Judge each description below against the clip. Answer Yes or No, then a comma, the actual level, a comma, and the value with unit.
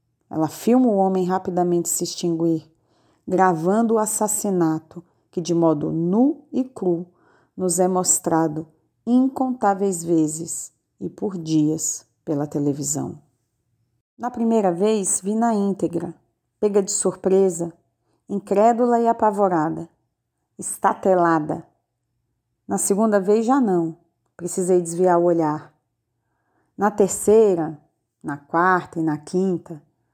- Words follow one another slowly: Yes, slow, 110 wpm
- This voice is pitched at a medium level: Yes, medium, 175 Hz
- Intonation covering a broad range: No, average, 4.4 semitones